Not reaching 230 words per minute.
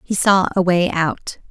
Yes: average, 200 wpm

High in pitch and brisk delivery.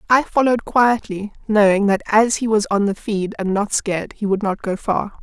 Yes: high, 210 Hz; fast, 220 wpm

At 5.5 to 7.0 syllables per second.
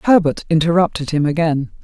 Yes: 5.8 syllables/s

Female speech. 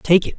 No: male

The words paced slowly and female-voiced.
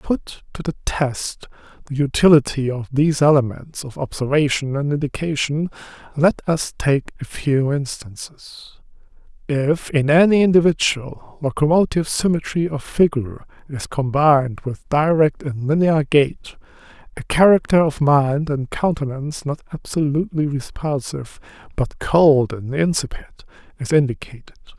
No: slow, 120 wpm; male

